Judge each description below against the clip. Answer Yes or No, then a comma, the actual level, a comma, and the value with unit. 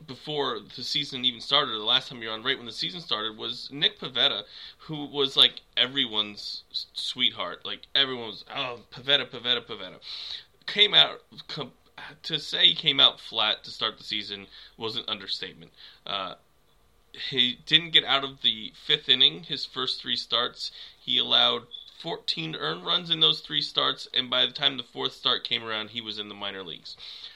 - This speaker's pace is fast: No, average, 180 wpm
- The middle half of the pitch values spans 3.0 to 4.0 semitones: No, average, 4.9 semitones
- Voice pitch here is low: Yes, low, 125 Hz